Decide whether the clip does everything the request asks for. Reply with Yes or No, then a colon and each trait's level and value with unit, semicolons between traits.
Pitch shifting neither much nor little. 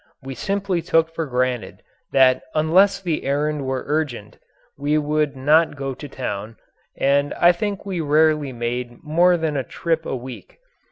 Yes: average, 3.7 semitones